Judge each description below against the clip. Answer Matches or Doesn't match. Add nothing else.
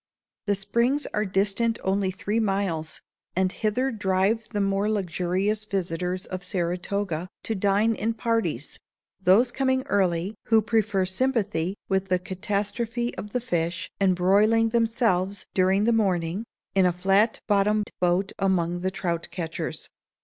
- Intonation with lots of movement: Doesn't match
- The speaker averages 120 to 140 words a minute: Matches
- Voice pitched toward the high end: Matches